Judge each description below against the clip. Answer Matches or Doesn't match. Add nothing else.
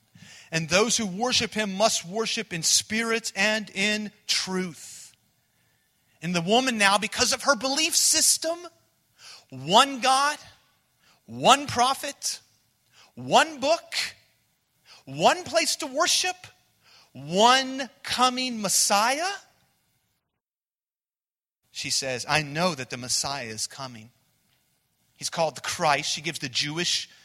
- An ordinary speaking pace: Doesn't match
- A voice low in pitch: Doesn't match